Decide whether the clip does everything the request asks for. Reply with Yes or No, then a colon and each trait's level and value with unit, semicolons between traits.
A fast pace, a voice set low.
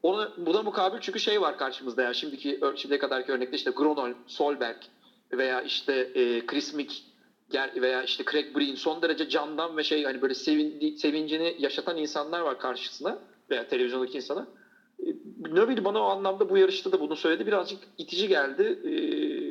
No: fast, 160 wpm; medium, 160 Hz